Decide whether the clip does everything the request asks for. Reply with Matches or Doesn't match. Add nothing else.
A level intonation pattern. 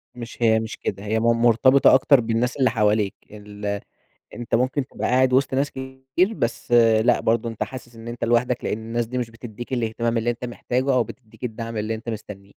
Matches